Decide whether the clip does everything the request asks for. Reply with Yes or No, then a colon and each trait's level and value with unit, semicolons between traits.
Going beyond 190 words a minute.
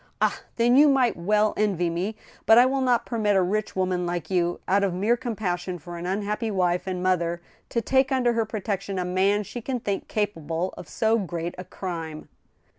Yes: average, 200 wpm